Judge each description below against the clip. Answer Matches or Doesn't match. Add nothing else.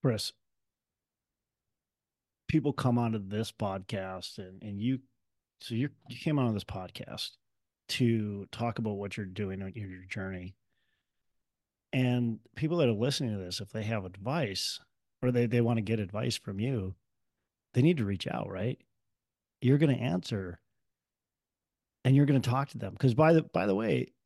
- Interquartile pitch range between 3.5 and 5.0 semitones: Matches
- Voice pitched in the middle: Doesn't match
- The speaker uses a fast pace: Doesn't match